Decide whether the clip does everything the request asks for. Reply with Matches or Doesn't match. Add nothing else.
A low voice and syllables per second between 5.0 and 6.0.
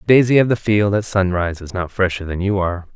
Doesn't match